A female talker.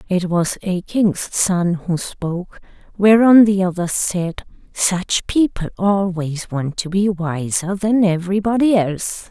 Yes: female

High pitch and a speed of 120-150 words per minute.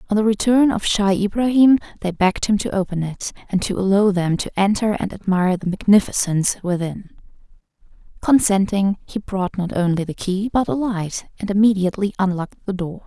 No: high, 195 Hz; average, 175 wpm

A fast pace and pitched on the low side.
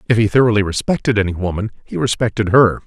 No: average, 190 wpm; low, 110 Hz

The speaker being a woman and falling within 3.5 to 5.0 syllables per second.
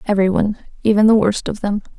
No: female; 7.5 syllables/s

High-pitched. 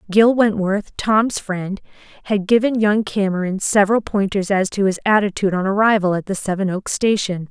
Yes: high, 200 Hz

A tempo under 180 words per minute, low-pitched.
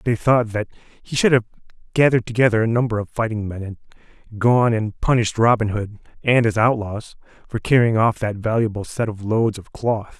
No: average, 195 wpm; low, 115 Hz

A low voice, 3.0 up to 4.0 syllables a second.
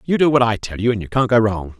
No: low, 115 Hz; 6.5 syllables/s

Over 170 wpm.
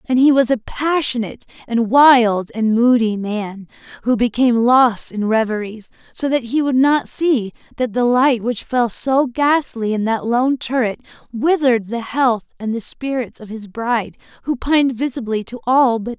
Yes: average, 180 wpm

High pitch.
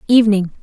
Yes: high, 210 Hz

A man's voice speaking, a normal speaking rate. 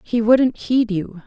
No: female; average, 190 wpm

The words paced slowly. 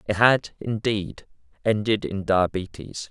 Yes: slow, 115 wpm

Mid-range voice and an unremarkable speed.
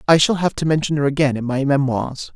No: medium, 145 Hz; fast, 255 wpm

